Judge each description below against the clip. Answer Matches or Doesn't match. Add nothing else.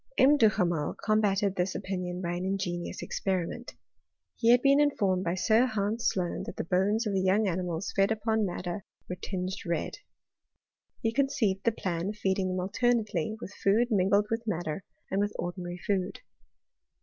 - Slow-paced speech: Doesn't match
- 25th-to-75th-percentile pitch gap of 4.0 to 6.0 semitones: Doesn't match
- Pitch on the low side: Doesn't match